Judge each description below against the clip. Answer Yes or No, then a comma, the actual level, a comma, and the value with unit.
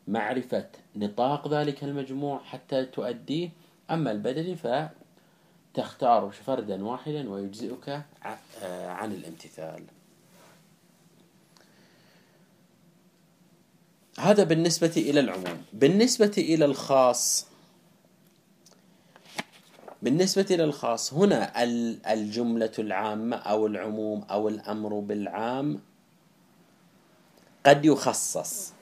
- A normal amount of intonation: No, wide, 7.6 semitones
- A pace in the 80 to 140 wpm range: No, average, 70 wpm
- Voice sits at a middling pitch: Yes, medium, 150 Hz